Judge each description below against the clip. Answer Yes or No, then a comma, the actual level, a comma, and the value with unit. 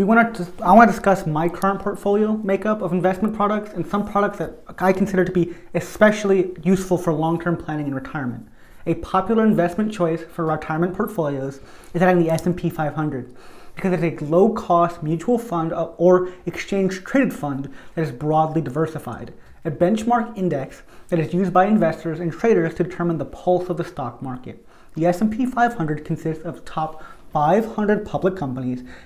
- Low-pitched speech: No, medium, 175 Hz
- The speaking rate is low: No, average, 170 wpm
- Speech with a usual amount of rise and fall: Yes, average, 3.4 semitones